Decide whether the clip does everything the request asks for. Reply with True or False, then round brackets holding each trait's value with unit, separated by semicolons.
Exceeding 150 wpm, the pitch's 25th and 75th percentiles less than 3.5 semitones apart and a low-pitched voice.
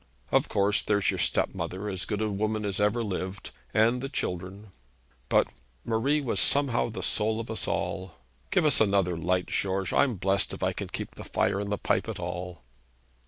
True (190 wpm; 2.9 semitones; 105 Hz)